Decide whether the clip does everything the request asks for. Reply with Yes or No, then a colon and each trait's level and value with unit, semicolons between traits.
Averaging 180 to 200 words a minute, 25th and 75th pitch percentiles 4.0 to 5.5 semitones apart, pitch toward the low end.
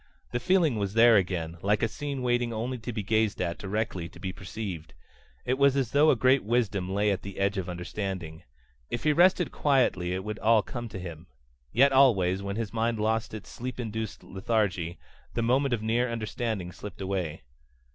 Yes: average, 195 wpm; average, 4.3 semitones; low, 110 Hz